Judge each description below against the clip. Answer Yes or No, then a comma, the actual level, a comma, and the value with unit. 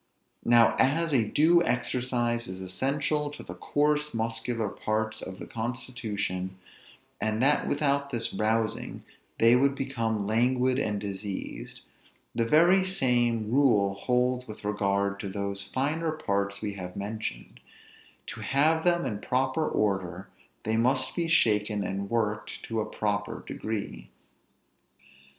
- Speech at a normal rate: No, slow, 130 wpm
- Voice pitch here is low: Yes, low, 115 Hz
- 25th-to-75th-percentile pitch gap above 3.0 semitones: Yes, average, 4.7 semitones